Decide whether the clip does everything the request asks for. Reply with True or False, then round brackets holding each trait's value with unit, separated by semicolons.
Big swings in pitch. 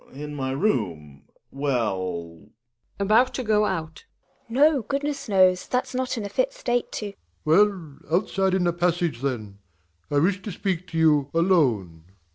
True (7.7 semitones)